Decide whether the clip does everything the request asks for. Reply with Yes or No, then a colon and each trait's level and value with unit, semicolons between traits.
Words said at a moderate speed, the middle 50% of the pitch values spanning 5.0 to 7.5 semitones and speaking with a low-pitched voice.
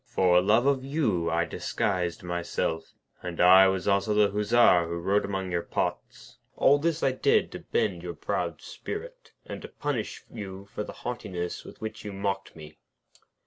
Yes: average, 175 wpm; average, 5.3 semitones; low, 100 Hz